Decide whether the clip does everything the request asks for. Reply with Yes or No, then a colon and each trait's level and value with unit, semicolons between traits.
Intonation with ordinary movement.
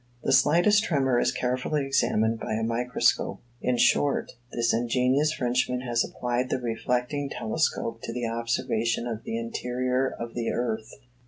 No: narrow, 2.0 semitones